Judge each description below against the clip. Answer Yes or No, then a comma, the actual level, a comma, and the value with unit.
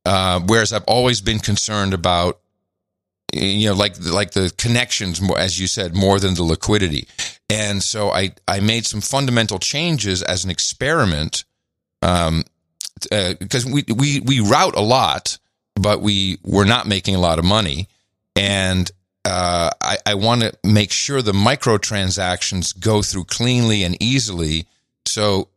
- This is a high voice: No, low, 100 Hz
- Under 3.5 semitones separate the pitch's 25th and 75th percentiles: Yes, average, 3.0 semitones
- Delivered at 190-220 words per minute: No, average, 155 wpm